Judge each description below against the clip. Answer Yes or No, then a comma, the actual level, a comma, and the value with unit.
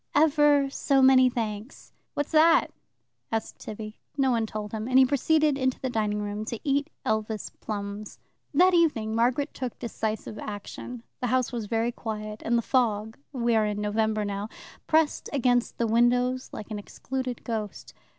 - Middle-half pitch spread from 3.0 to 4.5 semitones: Yes, average, 3.6 semitones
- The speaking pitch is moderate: No, high, 235 Hz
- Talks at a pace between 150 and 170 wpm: Yes, average, 165 wpm